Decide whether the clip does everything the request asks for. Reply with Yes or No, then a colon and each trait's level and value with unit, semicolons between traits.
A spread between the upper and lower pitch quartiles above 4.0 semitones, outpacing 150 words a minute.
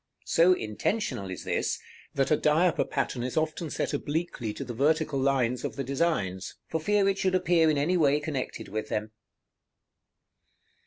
Yes: average, 4.8 semitones; average, 165 wpm